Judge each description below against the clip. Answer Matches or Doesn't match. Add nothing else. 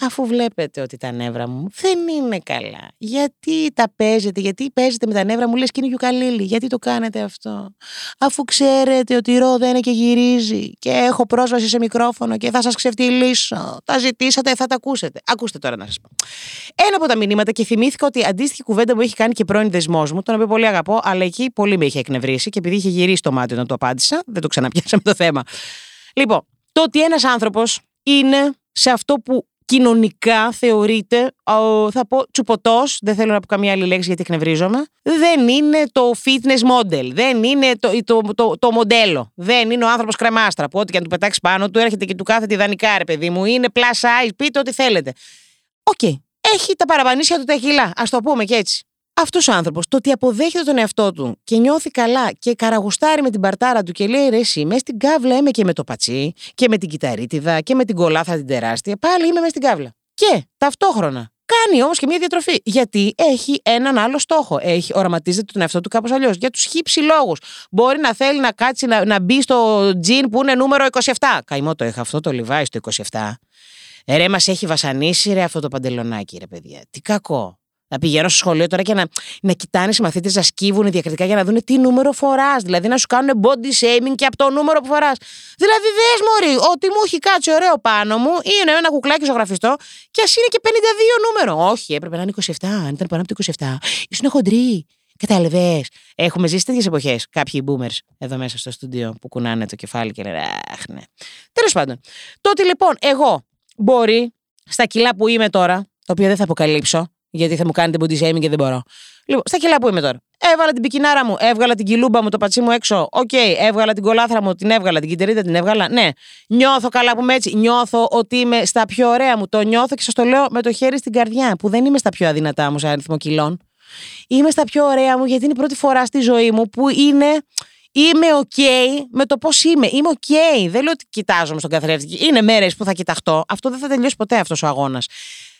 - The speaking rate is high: Matches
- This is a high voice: Matches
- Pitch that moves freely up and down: Matches